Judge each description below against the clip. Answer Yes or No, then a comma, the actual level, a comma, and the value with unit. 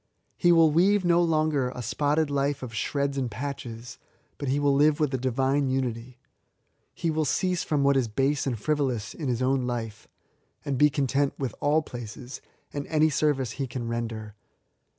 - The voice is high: No, medium, 140 Hz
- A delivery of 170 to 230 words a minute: Yes, average, 180 wpm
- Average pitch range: Yes, average, 3.2 semitones